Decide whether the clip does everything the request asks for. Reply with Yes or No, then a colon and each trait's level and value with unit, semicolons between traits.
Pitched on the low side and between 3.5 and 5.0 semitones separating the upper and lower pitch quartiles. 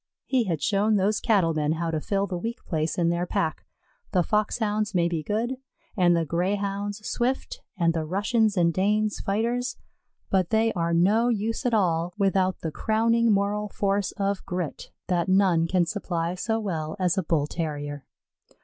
No: high, 195 Hz; average, 4.0 semitones